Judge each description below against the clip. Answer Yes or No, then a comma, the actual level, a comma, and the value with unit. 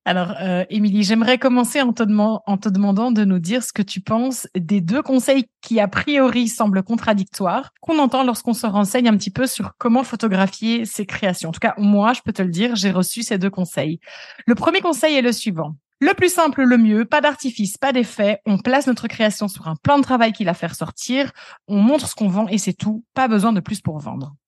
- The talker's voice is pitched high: Yes, high, 220 Hz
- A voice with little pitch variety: No, average, 4.2 semitones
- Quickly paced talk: Yes, fast, 225 wpm